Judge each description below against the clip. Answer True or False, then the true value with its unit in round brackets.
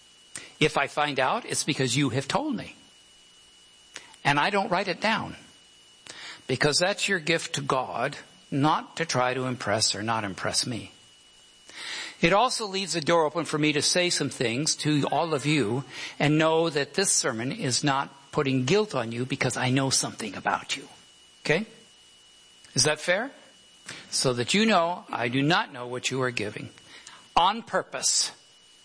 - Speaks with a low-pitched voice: False (145 Hz)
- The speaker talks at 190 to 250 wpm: False (170 wpm)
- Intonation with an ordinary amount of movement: True (4.2 semitones)